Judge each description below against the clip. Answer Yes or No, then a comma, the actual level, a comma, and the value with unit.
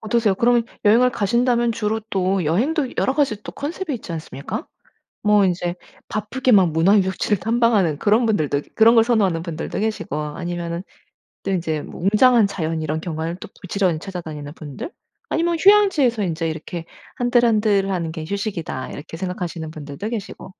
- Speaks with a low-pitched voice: No, high, 195 Hz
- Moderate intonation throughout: No, wide, 5.7 semitones